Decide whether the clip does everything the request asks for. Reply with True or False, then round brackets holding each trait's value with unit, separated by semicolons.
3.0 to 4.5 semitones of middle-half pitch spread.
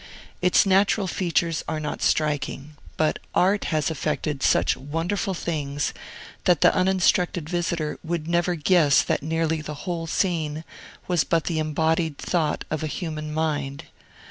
False (2.4 semitones)